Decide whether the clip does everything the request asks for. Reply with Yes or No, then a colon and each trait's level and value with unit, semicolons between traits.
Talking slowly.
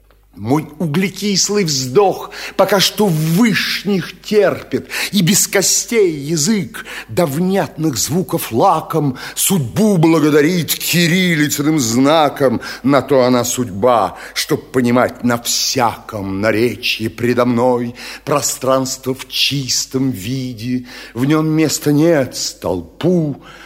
Yes: slow, 100 wpm